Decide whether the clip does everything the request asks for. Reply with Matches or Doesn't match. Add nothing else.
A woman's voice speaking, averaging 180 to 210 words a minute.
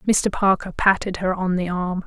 Matches